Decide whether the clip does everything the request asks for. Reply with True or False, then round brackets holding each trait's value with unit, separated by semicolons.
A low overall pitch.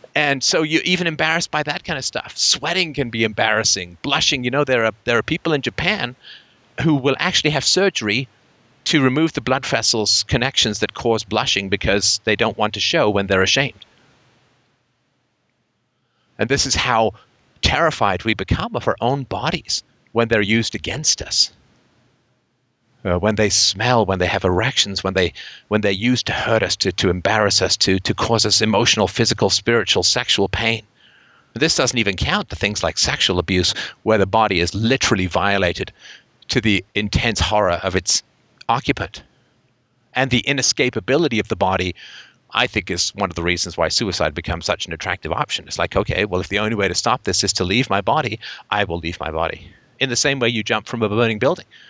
True (110 Hz)